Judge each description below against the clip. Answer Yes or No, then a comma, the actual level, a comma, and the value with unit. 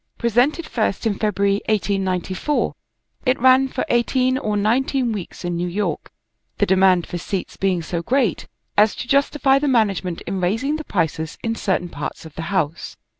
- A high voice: Yes, high, 205 Hz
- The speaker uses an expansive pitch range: Yes, wide, 5.9 semitones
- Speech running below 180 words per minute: Yes, average, 170 wpm